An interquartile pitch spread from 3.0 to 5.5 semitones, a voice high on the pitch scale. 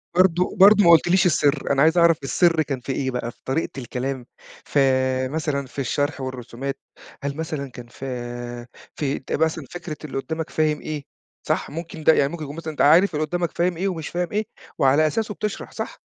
No: average, 3.7 semitones; medium, 155 Hz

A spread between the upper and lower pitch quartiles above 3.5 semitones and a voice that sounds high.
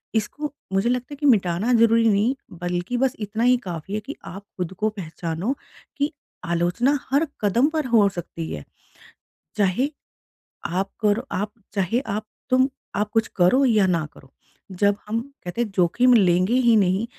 Yes: average, 5.2 semitones; high, 210 Hz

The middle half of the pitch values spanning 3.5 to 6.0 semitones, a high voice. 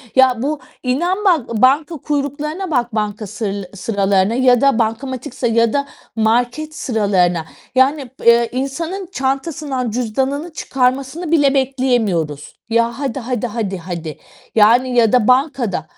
Yes: average, 4.0 semitones; very high, 250 Hz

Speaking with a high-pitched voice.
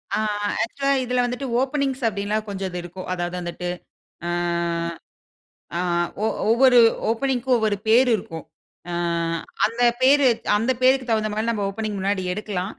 Yes: high, 225 Hz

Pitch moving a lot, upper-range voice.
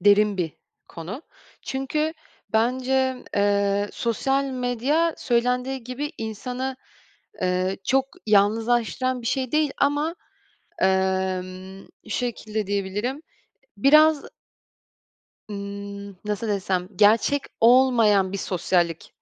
No: average, 4.7 semitones; high, 225 Hz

